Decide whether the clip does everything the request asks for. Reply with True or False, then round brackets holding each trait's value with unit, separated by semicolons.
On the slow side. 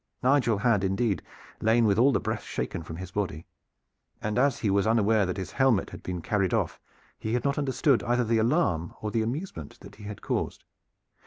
False (200 wpm)